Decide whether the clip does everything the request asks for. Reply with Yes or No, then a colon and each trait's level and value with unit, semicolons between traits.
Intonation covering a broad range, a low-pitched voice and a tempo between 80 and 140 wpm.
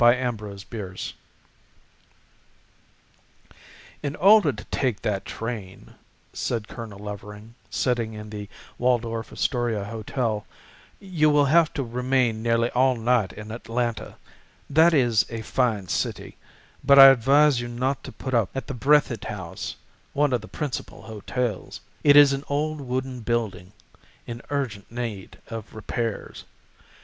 No: average, 3.7 semitones; low, 120 Hz; slow, 135 wpm